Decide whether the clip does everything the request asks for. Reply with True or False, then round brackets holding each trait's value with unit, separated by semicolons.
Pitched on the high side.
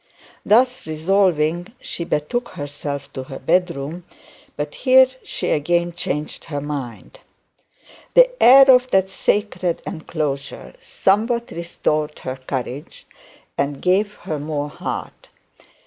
False (170 Hz)